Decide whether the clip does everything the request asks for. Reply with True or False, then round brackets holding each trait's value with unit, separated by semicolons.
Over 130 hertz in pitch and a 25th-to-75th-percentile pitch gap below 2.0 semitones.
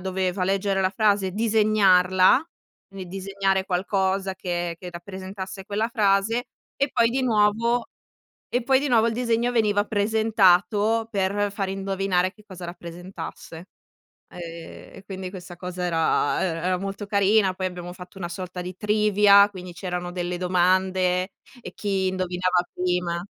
False (190 Hz; 2.4 semitones)